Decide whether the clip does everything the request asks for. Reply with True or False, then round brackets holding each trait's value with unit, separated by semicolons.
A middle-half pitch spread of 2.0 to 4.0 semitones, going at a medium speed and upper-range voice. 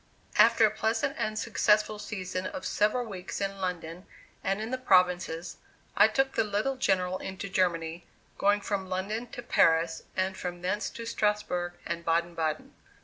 True (3.3 semitones; 160 wpm; 195 Hz)